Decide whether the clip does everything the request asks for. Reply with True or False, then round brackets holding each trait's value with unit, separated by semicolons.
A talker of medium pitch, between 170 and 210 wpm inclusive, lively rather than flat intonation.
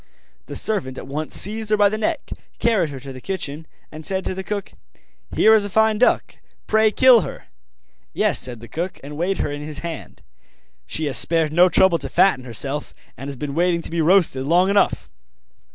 True (170 Hz; 205 wpm; 5.8 semitones)